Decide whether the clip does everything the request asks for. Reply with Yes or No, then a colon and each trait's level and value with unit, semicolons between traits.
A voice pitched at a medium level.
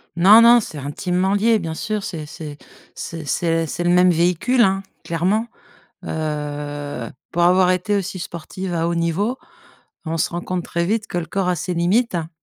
Yes: medium, 175 Hz